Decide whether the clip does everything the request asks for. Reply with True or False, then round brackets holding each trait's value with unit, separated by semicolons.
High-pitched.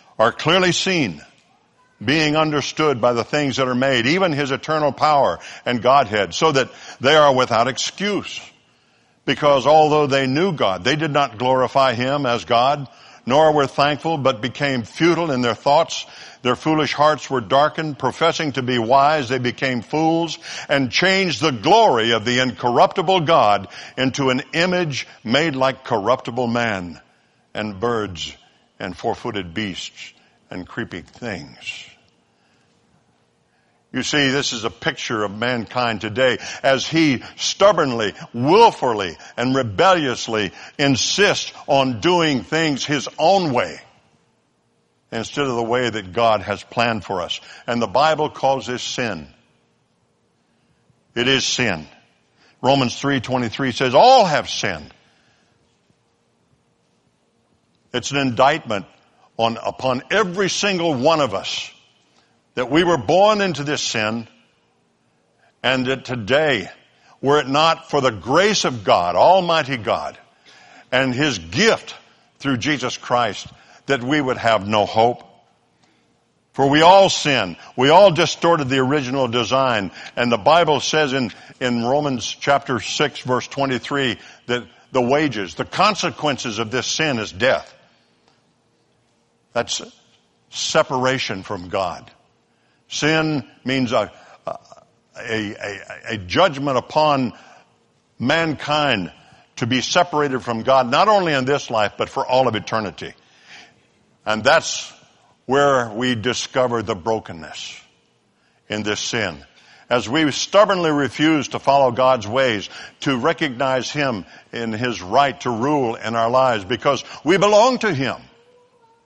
False (130 Hz)